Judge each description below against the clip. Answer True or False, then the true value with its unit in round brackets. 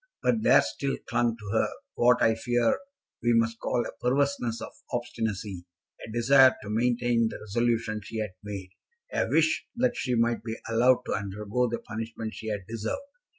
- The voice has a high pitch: False (115 Hz)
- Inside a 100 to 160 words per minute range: False (175 wpm)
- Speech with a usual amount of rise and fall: False (2.0 semitones)